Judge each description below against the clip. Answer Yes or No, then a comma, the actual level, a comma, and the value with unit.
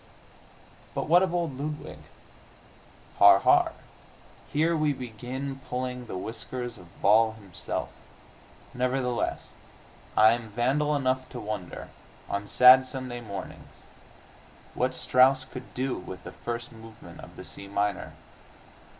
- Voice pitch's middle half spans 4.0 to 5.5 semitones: No, average, 3.0 semitones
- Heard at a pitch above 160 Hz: No, low, 125 Hz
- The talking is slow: Yes, slow, 125 wpm